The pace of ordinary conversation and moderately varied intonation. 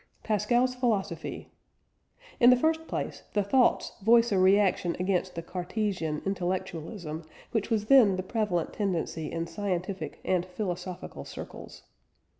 No: slow, 125 wpm; average, 3.8 semitones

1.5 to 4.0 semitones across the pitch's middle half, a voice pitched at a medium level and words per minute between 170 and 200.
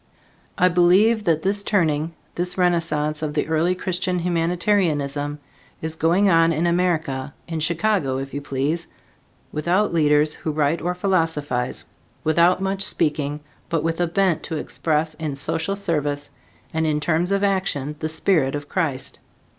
No: average, 3.1 semitones; medium, 165 Hz; average, 150 wpm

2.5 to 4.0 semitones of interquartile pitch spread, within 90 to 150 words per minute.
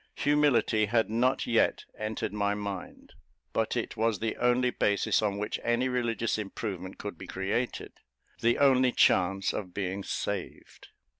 Yes: average, 3.2 semitones; average, 145 wpm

